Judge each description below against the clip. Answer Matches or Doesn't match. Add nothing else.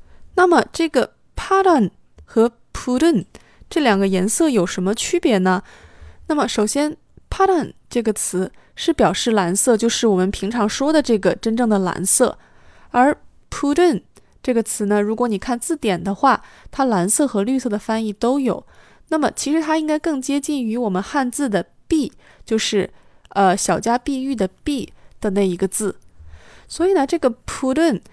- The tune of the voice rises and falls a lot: Matches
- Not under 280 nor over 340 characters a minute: Matches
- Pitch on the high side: Matches